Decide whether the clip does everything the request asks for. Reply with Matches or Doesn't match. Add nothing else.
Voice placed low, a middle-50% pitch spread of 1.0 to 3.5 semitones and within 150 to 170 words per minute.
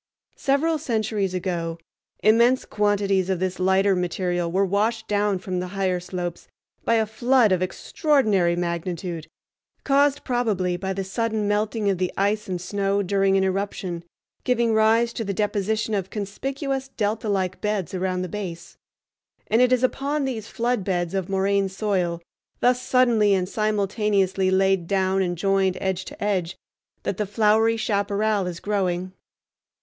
Doesn't match